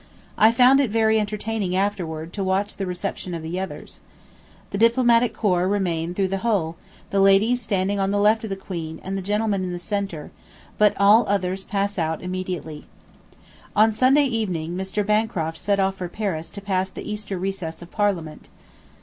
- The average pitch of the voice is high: Yes, high, 195 Hz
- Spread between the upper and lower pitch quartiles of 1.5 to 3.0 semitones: Yes, average, 2.7 semitones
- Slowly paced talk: No, average, 180 wpm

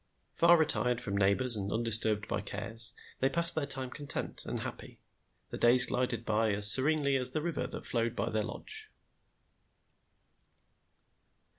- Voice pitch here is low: Yes, low, 125 Hz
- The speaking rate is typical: Yes, average, 150 wpm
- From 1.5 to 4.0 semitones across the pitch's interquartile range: No, average, 4.5 semitones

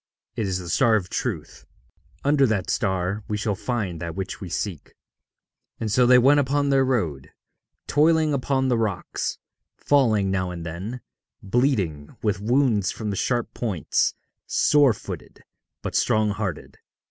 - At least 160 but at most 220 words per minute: No, average, 150 wpm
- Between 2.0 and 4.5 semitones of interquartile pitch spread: No, wide, 5.4 semitones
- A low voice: Yes, low, 110 Hz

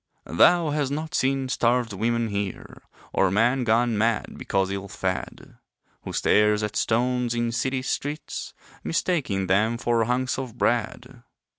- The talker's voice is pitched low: Yes, low, 120 Hz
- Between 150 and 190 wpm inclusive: No, average, 140 wpm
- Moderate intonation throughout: Yes, average, 3.5 semitones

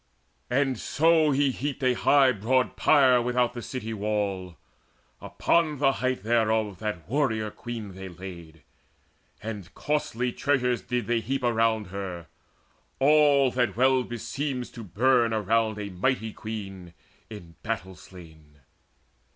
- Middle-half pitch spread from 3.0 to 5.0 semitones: Yes, average, 4.5 semitones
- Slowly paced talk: Yes, slow, 130 wpm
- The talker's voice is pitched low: Yes, low, 115 Hz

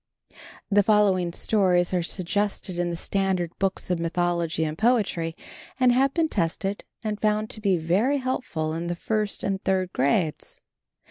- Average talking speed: Yes, average, 155 wpm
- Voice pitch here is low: No, high, 190 Hz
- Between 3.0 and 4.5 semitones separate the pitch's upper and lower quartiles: Yes, average, 3.6 semitones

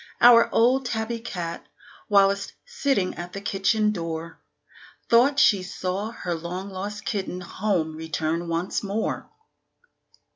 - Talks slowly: Yes, slow, 120 wpm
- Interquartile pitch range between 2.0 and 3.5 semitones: No, average, 4.2 semitones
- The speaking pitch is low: No, high, 195 Hz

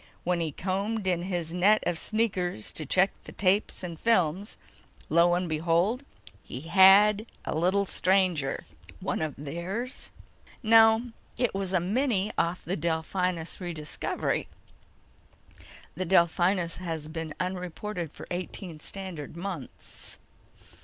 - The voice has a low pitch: No, medium, 180 Hz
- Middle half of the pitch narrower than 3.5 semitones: Yes, average, 3.0 semitones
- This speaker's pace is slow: Yes, slow, 125 wpm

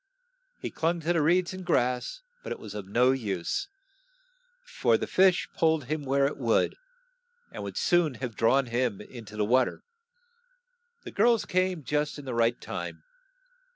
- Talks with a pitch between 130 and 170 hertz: Yes, low, 135 Hz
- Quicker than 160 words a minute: Yes, average, 175 wpm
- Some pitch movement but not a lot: No, wide, 6.1 semitones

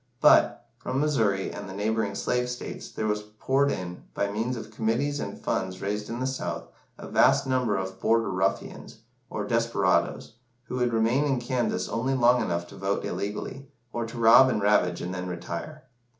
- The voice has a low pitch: Yes, low, 110 Hz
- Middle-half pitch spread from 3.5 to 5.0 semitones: Yes, average, 4.1 semitones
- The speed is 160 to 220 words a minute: Yes, average, 180 wpm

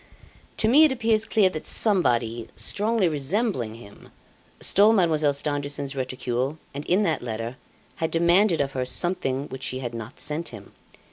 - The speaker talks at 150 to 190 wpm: Yes, average, 155 wpm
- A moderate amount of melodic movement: No, wide, 7.1 semitones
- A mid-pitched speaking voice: Yes, medium, 150 Hz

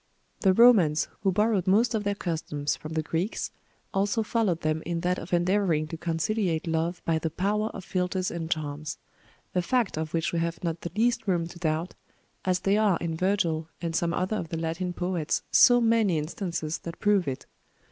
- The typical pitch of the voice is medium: Yes, medium, 175 Hz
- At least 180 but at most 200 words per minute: Yes, average, 195 wpm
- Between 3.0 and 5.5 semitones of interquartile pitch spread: Yes, average, 3.6 semitones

